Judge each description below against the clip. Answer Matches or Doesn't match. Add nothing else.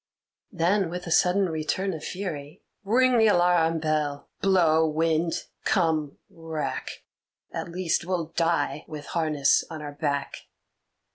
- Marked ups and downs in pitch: Doesn't match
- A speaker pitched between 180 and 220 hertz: Doesn't match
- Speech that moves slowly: Matches